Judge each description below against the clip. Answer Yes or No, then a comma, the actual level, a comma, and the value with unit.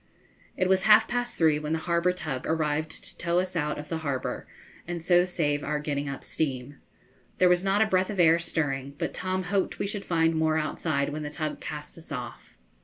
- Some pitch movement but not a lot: Yes, average, 3.4 semitones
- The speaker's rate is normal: No, fast, 215 wpm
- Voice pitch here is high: No, medium, 160 Hz